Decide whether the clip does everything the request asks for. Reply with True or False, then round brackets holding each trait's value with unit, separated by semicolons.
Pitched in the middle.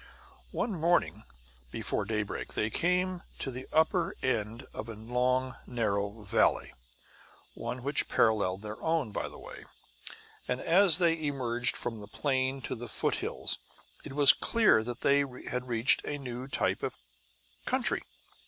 False (125 Hz)